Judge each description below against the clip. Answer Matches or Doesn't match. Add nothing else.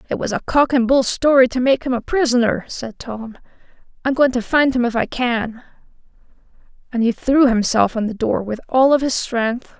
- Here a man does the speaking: Doesn't match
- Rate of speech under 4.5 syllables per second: Doesn't match